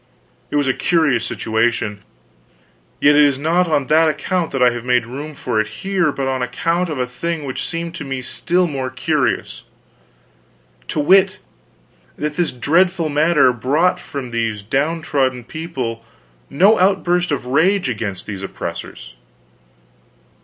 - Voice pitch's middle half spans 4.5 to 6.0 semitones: Yes, average, 5.2 semitones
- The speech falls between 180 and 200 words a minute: No, average, 150 wpm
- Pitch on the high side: No, medium, 145 Hz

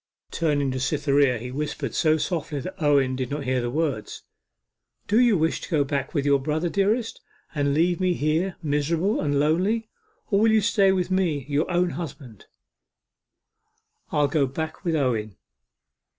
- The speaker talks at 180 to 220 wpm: No, average, 165 wpm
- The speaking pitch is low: No, medium, 150 Hz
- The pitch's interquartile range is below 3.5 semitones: No, average, 4.2 semitones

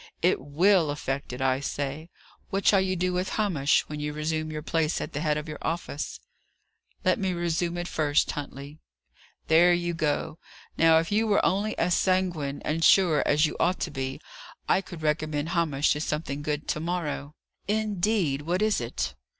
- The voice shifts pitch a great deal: No, average, 3.4 semitones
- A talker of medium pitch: Yes, medium, 160 Hz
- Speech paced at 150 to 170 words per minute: No, average, 185 wpm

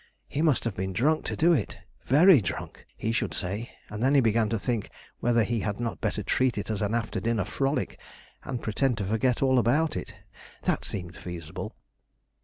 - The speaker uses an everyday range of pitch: Yes, average, 4.2 semitones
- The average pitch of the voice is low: Yes, low, 115 Hz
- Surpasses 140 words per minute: Yes, average, 200 wpm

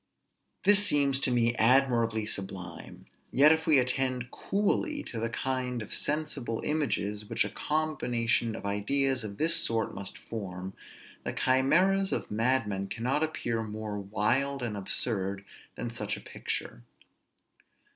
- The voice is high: No, low, 120 Hz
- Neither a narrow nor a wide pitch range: Yes, average, 4.7 semitones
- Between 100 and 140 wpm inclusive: Yes, slow, 135 wpm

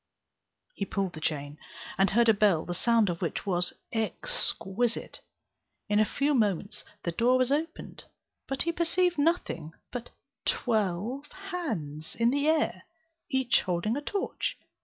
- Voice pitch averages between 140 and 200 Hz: No, high, 230 Hz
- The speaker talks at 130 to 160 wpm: Yes, average, 145 wpm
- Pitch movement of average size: No, wide, 7.9 semitones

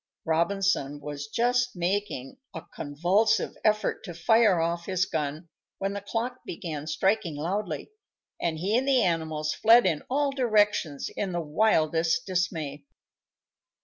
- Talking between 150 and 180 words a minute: No, slow, 135 wpm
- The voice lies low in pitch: No, medium, 180 Hz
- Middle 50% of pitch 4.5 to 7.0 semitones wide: Yes, average, 5.2 semitones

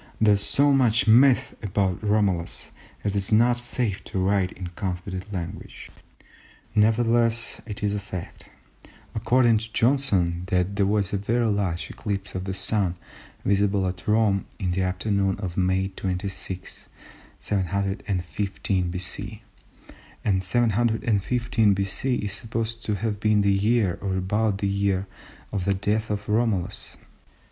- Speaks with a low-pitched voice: Yes, low, 100 Hz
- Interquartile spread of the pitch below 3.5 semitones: Yes, average, 2.8 semitones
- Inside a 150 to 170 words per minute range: No, average, 140 wpm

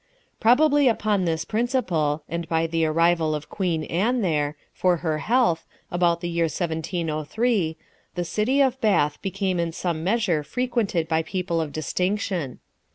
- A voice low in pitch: No, medium, 175 Hz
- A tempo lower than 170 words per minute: Yes, average, 155 wpm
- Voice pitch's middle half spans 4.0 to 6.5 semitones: Yes, average, 4.8 semitones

